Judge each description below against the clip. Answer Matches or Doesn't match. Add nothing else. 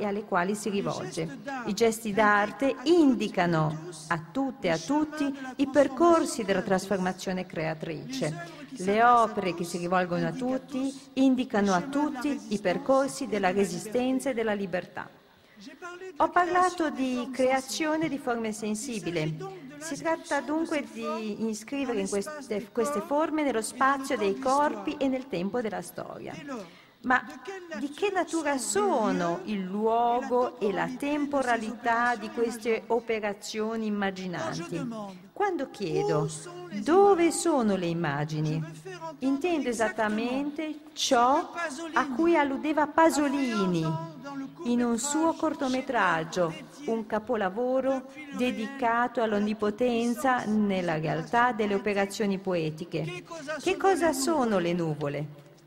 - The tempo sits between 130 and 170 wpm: Doesn't match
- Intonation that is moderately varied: Doesn't match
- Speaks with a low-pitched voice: Doesn't match